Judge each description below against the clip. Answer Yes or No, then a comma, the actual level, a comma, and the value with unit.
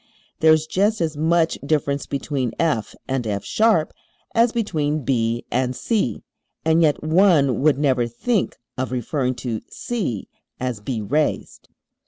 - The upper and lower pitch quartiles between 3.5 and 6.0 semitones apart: Yes, average, 4.6 semitones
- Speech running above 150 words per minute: No, average, 140 wpm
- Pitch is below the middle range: No, medium, 145 Hz